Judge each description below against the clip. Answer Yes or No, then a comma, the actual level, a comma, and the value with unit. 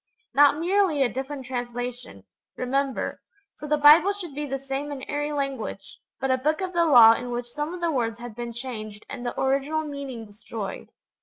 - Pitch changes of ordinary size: Yes, average, 3.5 semitones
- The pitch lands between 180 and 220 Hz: No, very high, 270 Hz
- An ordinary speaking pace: Yes, average, 190 wpm